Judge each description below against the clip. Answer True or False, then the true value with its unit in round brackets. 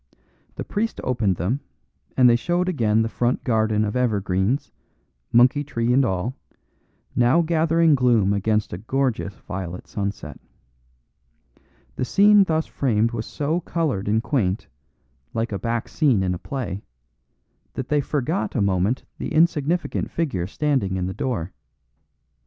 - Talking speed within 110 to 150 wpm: True (140 wpm)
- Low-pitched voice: True (120 Hz)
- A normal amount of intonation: False (6.2 semitones)